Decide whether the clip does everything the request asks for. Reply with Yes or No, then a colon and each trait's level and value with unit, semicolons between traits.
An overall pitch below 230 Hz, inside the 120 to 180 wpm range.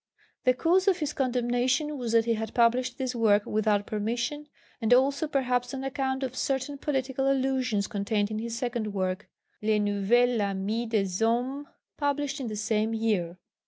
No: high, 240 Hz; average, 165 wpm